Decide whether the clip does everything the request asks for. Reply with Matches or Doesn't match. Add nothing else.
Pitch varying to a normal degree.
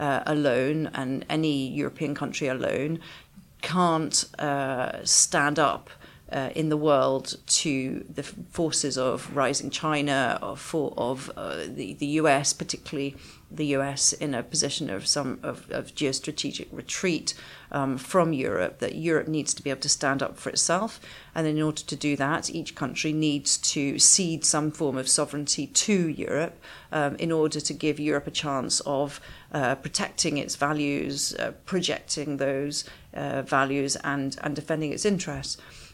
Doesn't match